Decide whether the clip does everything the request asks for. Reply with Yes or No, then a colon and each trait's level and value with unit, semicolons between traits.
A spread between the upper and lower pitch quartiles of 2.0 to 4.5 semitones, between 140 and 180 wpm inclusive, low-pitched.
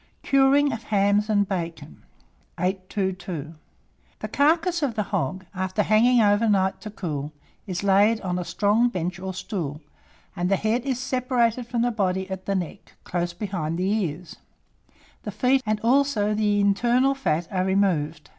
No: average, 4.2 semitones; average, 160 wpm; high, 200 Hz